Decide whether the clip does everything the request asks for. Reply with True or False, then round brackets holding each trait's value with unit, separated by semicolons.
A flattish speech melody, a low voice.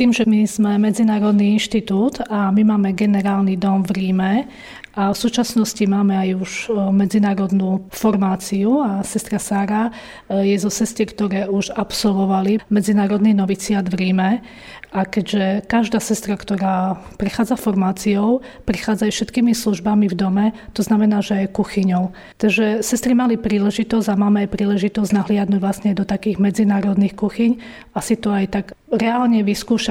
False (1.9 semitones; 205 Hz)